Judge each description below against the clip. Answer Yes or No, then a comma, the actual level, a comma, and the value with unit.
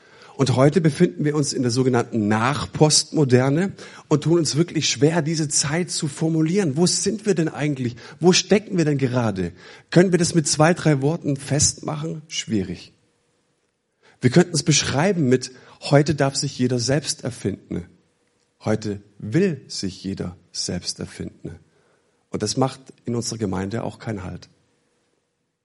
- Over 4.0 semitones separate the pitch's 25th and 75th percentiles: Yes, average, 4.6 semitones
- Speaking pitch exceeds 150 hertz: No, medium, 145 Hz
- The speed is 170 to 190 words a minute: No, average, 145 wpm